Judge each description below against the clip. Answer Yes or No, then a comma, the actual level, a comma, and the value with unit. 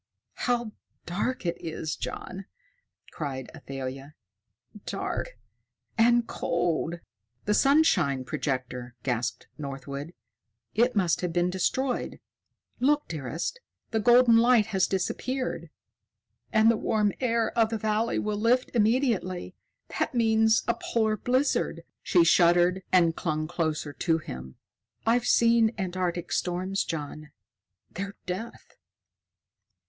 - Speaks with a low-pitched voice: No, high, 190 Hz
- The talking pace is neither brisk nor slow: No, slow, 110 wpm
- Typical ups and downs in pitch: No, wide, 6.3 semitones